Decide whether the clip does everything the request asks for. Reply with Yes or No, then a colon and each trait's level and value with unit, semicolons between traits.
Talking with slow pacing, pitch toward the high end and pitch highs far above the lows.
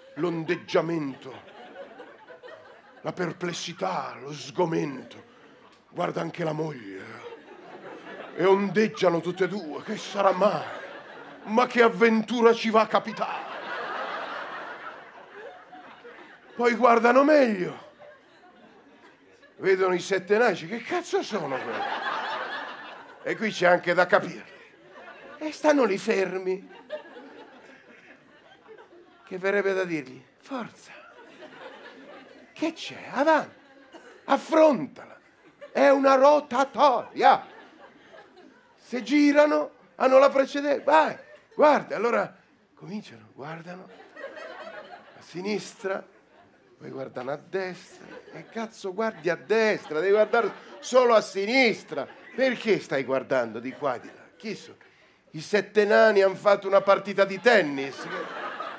Yes: slow, 105 wpm; high, 210 Hz; wide, 7.0 semitones